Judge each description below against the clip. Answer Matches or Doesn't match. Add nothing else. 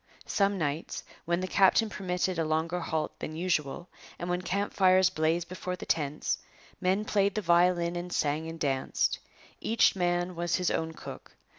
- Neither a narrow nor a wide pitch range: Doesn't match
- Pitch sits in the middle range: Matches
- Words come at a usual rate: Matches